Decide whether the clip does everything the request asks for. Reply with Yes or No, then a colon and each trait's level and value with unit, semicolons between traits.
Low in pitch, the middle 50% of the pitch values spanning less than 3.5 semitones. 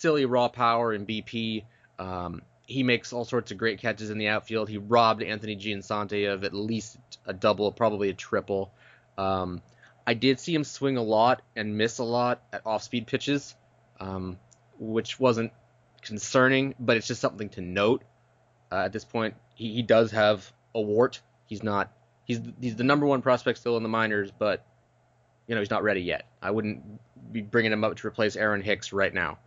Yes: low, 110 Hz; narrow, 2.5 semitones